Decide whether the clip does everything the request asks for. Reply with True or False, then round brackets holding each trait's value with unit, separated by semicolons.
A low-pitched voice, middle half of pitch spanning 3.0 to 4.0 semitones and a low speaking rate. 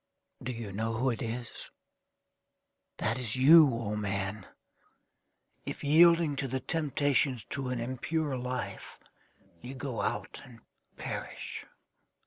True (125 Hz; 3.6 semitones; 120 wpm)